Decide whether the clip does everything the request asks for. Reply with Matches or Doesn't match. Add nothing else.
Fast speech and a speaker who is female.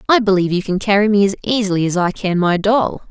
Matches